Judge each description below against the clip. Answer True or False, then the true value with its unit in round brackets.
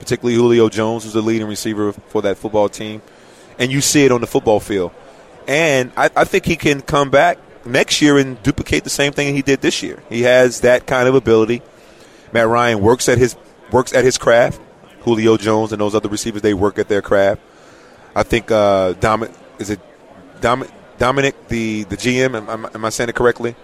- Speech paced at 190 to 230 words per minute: True (205 wpm)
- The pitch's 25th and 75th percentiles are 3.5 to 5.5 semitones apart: False (2.8 semitones)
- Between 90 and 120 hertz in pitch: True (115 Hz)